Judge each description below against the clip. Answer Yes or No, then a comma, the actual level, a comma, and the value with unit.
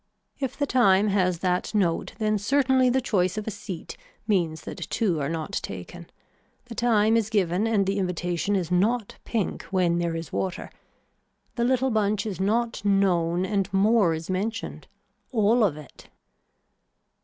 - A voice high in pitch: Yes, high, 200 Hz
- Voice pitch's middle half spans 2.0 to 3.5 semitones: No, average, 4.0 semitones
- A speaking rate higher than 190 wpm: No, average, 160 wpm